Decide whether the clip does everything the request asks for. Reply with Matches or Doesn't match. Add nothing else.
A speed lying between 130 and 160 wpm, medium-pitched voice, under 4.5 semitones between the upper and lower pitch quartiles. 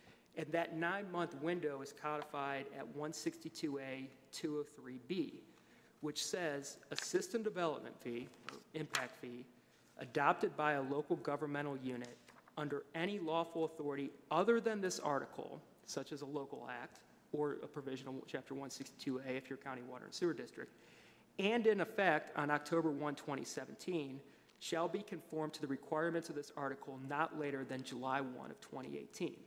Matches